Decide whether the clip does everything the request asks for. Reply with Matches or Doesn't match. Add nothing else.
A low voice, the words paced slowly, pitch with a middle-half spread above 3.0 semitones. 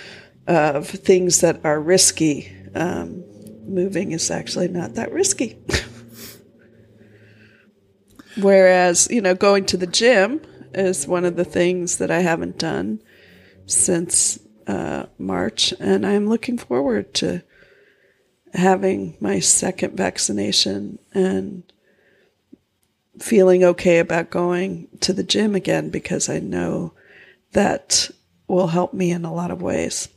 Doesn't match